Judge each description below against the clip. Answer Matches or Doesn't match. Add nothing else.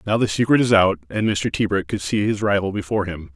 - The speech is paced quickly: Matches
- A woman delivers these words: Doesn't match